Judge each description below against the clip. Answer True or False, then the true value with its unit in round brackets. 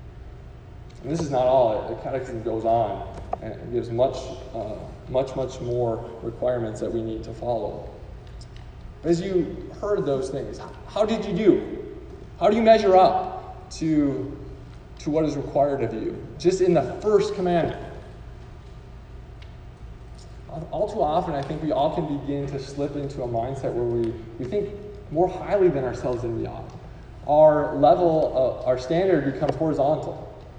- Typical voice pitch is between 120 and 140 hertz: True (135 Hz)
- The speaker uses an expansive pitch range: True (5.7 semitones)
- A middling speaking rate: True (155 wpm)